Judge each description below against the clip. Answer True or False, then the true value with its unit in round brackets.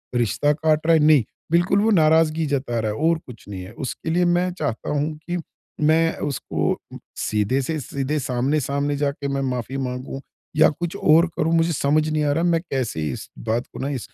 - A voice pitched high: False (150 Hz)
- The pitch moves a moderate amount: True (3.7 semitones)